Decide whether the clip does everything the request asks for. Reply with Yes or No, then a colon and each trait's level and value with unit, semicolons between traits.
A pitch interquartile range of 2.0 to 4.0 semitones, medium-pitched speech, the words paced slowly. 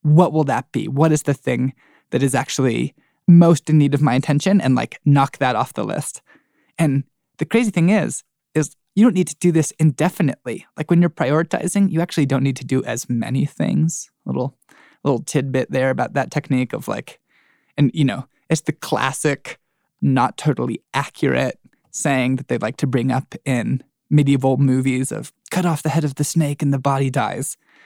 No: average, 3.3 semitones; medium, 145 Hz; average, 195 wpm